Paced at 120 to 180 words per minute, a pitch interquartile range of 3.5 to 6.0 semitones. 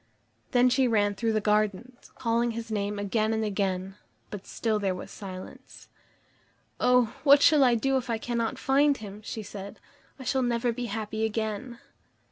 No: average, 170 wpm; average, 3.0 semitones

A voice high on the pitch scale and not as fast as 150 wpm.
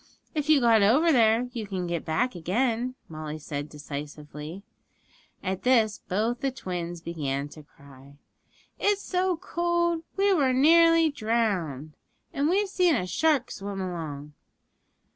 Yes: high, 215 Hz; average, 140 wpm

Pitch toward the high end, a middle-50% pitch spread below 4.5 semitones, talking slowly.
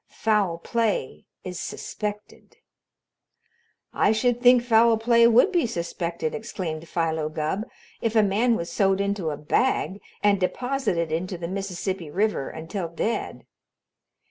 No: high, 200 Hz; average, 5.2 semitones; slow, 130 wpm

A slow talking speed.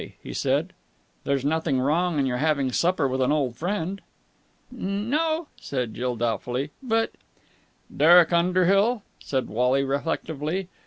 Yes: slow, 130 wpm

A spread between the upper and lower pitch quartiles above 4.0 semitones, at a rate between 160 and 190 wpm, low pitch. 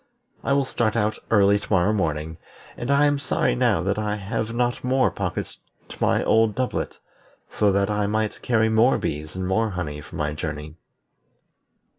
Yes: average, 4.4 semitones; average, 175 wpm; low, 105 Hz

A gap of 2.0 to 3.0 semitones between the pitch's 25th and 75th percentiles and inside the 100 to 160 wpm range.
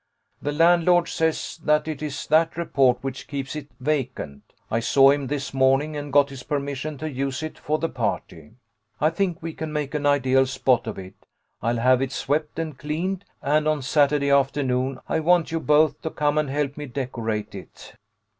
No: narrow, 2.6 semitones; average, 190 wpm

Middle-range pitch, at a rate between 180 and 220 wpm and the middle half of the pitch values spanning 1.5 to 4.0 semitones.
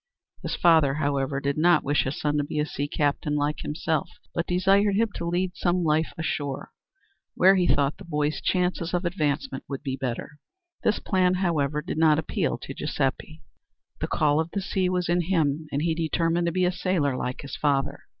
Yes: medium, 160 Hz; average, 200 wpm; average, 3.6 semitones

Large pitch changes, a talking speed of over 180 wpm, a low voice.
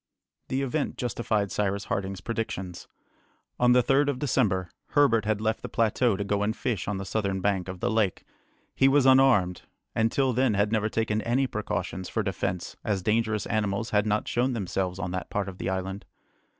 No: average, 3.6 semitones; average, 190 wpm; low, 105 Hz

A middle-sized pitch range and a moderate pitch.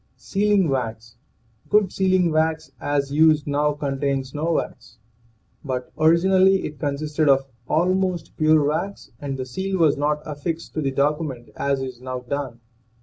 Yes: average, 3.4 semitones; medium, 150 Hz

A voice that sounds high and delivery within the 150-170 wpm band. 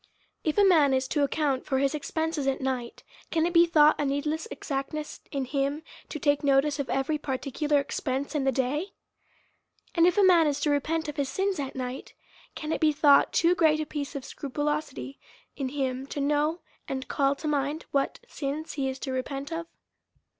No: very high, 290 Hz; average, 200 wpm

